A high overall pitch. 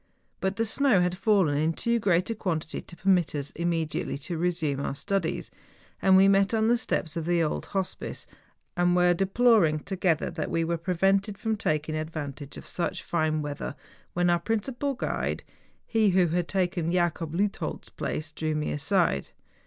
No: medium, 175 Hz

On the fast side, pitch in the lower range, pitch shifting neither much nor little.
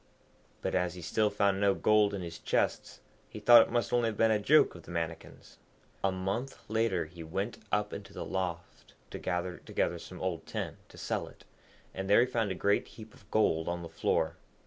Yes: fast, 215 wpm; low, 100 Hz; average, 3.6 semitones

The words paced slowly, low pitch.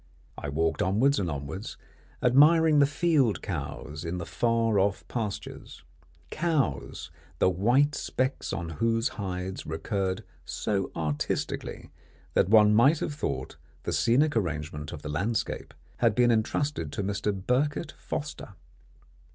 Yes: slow, 130 wpm; low, 105 Hz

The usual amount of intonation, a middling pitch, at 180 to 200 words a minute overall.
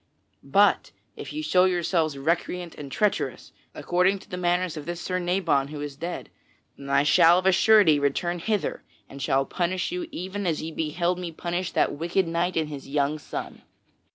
Yes: average, 3.2 semitones; medium, 175 Hz; average, 185 wpm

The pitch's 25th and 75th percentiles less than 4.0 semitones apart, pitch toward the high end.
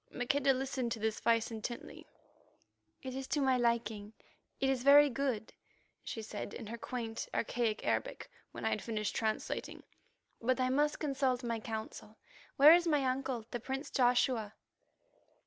Yes: average, 3.2 semitones; high, 245 Hz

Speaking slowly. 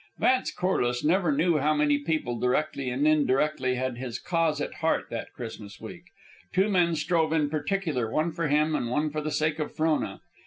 No: average, 190 wpm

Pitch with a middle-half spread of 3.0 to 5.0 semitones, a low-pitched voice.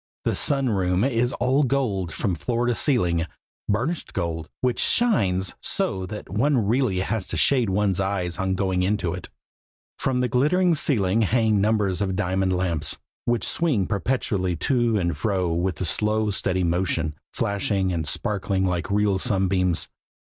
Yes: average, 4.5 semitones; low, 100 Hz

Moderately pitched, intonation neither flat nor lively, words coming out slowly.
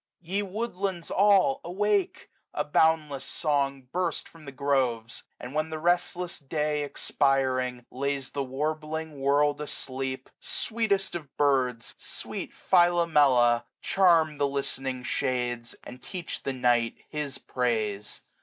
Yes: medium, 145 Hz; average, 4.7 semitones; slow, 125 wpm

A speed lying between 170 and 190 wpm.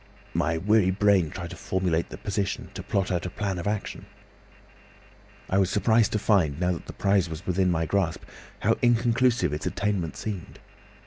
Yes: average, 180 wpm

